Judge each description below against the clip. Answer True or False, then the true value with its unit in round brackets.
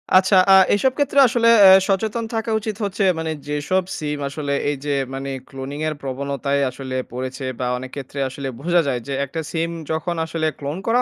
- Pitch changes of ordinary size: False (5.7 semitones)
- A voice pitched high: False (150 Hz)